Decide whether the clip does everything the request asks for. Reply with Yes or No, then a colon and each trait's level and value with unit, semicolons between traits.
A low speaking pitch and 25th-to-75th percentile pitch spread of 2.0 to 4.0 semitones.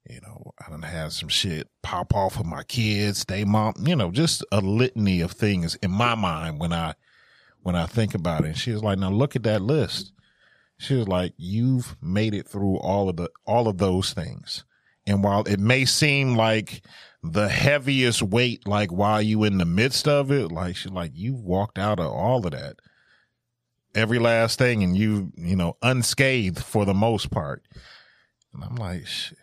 No: low, 105 Hz; average, 4.4 semitones